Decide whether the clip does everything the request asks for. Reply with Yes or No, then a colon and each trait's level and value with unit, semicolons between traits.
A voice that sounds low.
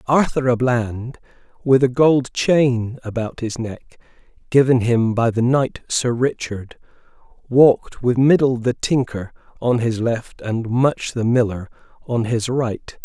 Yes: low, 120 Hz